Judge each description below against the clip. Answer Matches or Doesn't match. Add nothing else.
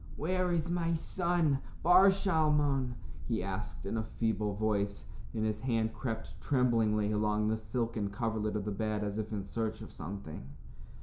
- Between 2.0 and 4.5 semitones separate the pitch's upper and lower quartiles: Doesn't match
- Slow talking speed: Doesn't match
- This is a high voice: Doesn't match